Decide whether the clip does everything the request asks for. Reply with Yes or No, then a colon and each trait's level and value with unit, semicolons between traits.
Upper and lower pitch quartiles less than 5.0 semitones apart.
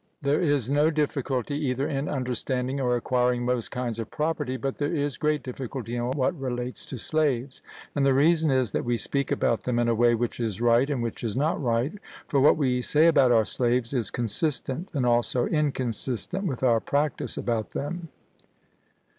Yes: average, 3.2 semitones